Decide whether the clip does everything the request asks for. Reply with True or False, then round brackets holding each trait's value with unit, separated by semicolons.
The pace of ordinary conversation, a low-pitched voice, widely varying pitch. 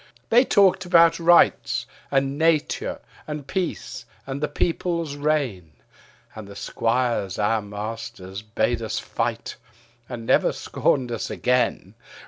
False (120 wpm; 130 Hz; 6.7 semitones)